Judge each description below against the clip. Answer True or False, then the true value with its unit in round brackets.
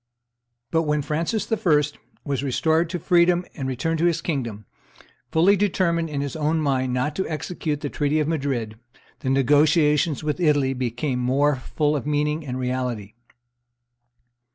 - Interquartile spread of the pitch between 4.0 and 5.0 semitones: False (3.6 semitones)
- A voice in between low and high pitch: True (150 Hz)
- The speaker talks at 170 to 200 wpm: False (155 wpm)